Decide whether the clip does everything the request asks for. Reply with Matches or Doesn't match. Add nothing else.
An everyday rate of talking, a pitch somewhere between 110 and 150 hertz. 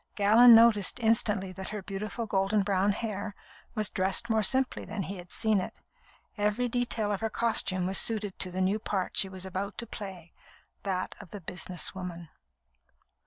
Doesn't match